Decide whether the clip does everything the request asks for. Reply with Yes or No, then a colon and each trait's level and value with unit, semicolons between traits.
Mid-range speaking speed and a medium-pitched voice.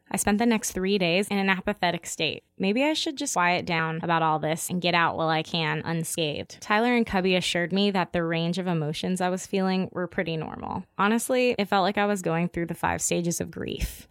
No: fast, 235 wpm; medium, 180 Hz